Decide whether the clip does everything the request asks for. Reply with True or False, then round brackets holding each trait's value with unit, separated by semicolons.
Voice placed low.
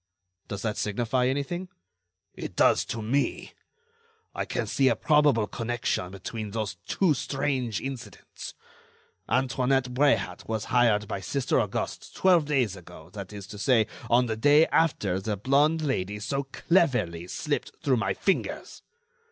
True (120 Hz)